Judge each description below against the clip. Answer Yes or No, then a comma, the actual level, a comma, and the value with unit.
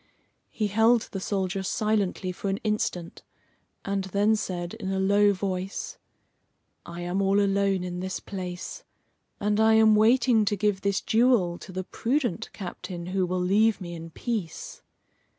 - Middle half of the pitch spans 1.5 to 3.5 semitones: Yes, average, 2.8 semitones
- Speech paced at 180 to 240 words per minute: No, average, 155 wpm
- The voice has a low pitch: No, high, 195 Hz